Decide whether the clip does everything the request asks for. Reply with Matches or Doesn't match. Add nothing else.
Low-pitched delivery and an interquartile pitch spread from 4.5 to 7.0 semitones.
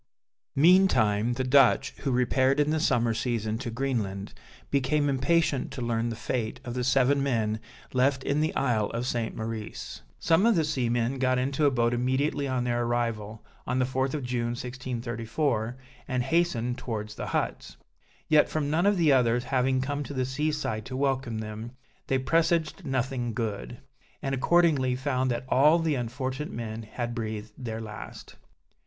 Doesn't match